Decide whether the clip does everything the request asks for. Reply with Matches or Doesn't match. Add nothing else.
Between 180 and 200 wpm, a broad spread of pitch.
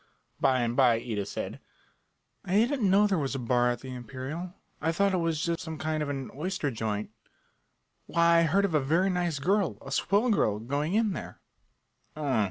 Matches